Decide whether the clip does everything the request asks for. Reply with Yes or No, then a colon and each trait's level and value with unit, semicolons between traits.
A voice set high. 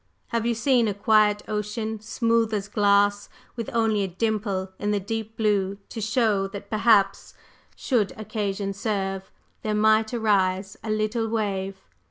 Yes: high, 210 Hz